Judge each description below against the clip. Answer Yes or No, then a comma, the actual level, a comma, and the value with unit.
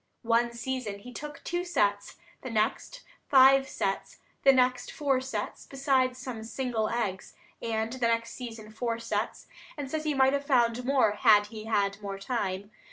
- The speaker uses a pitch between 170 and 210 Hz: No, high, 235 Hz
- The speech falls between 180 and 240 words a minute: No, average, 165 wpm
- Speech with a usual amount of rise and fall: Yes, average, 3.5 semitones